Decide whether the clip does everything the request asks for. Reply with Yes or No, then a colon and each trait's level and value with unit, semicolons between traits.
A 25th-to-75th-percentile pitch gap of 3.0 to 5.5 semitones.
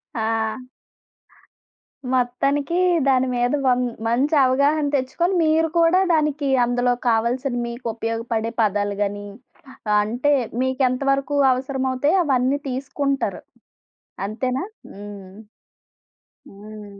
Yes: average, 3.5 semitones